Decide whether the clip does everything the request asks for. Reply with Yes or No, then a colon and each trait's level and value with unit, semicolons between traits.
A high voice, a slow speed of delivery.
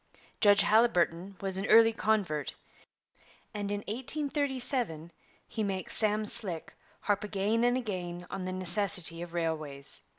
Yes: high, 200 Hz; slow, 130 wpm